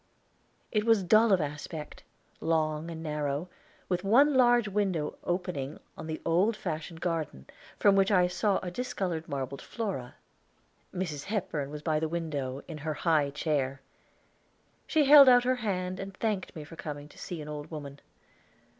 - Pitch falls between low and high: Yes, medium, 165 Hz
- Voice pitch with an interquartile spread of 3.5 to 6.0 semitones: Yes, average, 4.8 semitones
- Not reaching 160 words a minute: No, average, 165 wpm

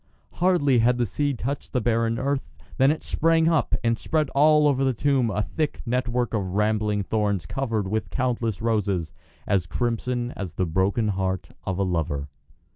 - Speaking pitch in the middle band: No, low, 115 Hz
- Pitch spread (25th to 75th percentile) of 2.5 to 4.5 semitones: No, average, 5.1 semitones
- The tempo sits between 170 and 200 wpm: Yes, average, 175 wpm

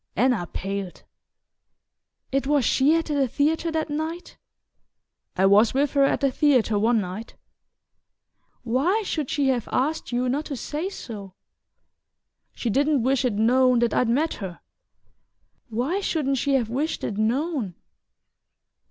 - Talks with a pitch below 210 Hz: No, very high, 260 Hz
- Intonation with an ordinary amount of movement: Yes, average, 4.7 semitones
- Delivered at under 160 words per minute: Yes, average, 145 wpm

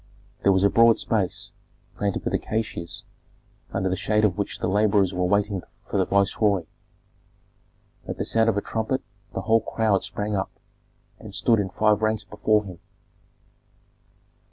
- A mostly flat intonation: Yes, narrow, 2.1 semitones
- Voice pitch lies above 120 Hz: No, low, 105 Hz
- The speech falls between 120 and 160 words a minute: Yes, average, 155 wpm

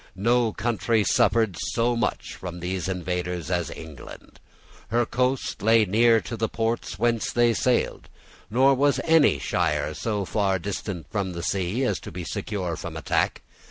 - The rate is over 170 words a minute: No, average, 160 wpm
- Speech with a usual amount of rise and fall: Yes, average, 4.7 semitones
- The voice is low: Yes, low, 105 Hz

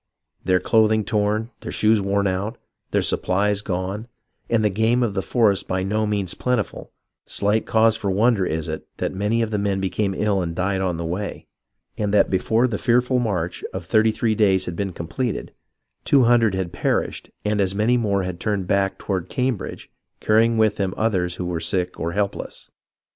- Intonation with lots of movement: No, average, 2.9 semitones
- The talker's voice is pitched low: Yes, low, 100 Hz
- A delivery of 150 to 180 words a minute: No, average, 190 wpm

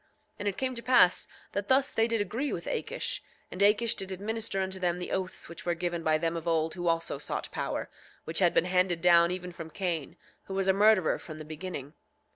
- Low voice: No, medium, 180 Hz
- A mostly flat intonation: No, average, 3.3 semitones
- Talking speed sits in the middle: No, fast, 230 wpm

